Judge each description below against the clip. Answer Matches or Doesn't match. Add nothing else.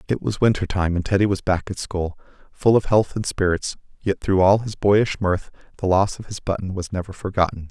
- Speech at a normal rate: Doesn't match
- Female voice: Doesn't match